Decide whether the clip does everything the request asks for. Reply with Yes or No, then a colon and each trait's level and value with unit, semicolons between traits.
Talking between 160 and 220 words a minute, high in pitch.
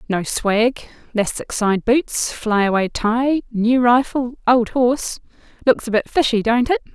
No: average, 145 wpm; high, 235 Hz